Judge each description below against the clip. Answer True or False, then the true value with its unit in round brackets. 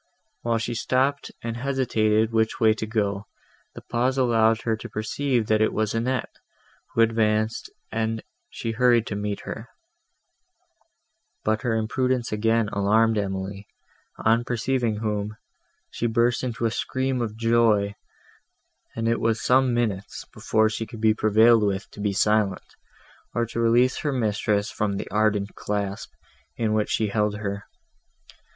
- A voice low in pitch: True (110 Hz)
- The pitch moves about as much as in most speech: False (1.8 semitones)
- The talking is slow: False (150 wpm)